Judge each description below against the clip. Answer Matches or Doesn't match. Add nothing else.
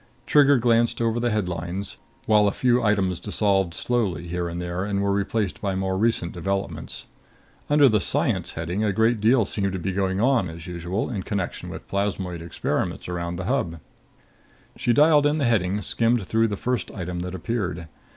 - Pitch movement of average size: Matches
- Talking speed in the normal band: Matches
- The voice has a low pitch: Matches